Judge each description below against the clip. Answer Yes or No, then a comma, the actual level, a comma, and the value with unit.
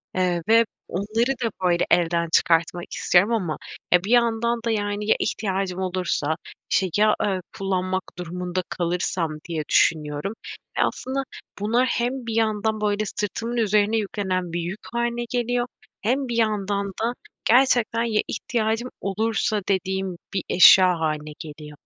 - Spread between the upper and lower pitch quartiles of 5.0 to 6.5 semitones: No, average, 4.1 semitones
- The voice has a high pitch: Yes, high, 200 Hz